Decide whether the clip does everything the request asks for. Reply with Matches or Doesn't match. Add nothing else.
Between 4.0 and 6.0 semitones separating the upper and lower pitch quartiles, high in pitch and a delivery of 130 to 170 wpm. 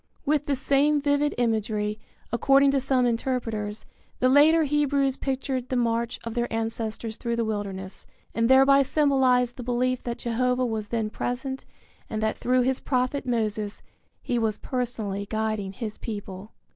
Doesn't match